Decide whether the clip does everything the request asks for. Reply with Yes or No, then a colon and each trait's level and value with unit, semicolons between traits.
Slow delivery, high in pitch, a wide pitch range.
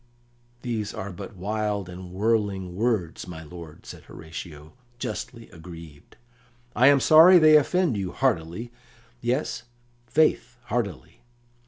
No: slow, 120 wpm; low, 105 Hz; wide, 5.7 semitones